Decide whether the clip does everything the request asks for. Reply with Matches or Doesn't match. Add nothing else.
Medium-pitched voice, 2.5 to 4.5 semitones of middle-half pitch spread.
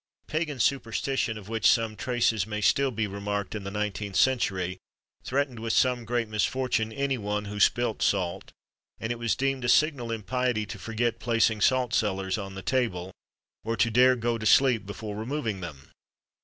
Doesn't match